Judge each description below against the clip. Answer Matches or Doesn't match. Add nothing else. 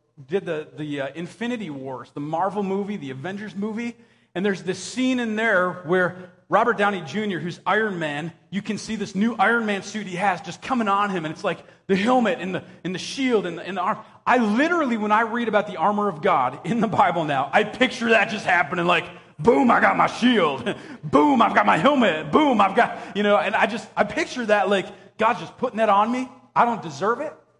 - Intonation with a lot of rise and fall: Doesn't match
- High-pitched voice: Matches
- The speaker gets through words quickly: Matches